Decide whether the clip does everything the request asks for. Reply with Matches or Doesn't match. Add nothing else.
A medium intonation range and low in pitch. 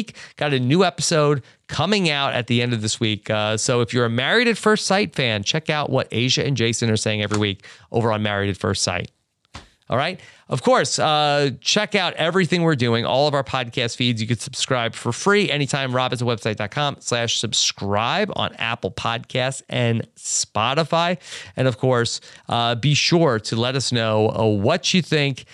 Matches